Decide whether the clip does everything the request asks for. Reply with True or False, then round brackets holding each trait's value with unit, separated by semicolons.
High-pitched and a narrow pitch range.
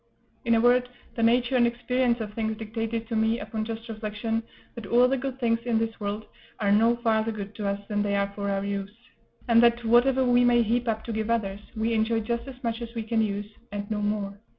True (225 Hz; 2.1 semitones)